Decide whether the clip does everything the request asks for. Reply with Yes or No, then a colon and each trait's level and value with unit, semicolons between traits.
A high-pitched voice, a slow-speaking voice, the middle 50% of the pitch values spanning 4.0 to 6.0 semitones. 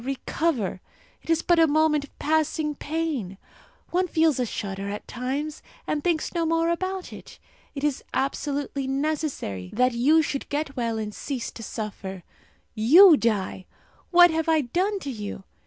No: very high, 290 Hz; average, 160 wpm; wide, 5.5 semitones